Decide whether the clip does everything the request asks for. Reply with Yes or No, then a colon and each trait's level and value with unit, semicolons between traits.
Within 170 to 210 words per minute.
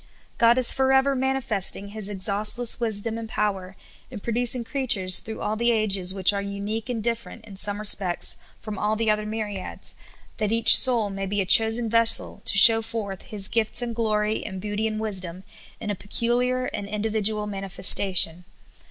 Yes: average, 180 wpm